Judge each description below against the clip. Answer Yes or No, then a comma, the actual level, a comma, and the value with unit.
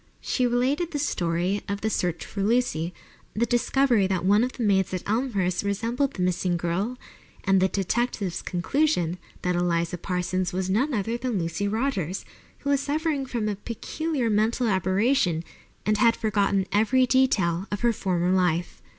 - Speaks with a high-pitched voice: Yes, high, 205 Hz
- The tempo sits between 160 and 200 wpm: Yes, average, 165 wpm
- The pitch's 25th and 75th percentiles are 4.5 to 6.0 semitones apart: Yes, average, 5.1 semitones